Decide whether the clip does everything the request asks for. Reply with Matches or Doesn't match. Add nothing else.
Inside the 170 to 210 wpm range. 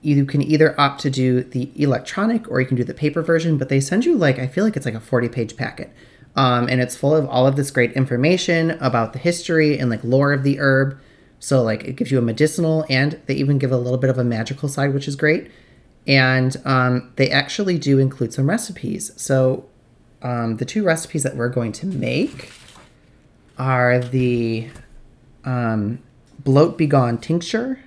Matches